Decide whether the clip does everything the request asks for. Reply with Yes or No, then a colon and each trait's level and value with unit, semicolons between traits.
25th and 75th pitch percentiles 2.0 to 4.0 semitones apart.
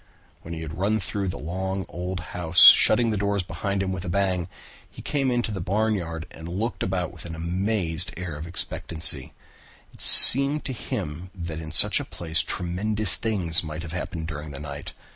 Yes: average, 3.5 semitones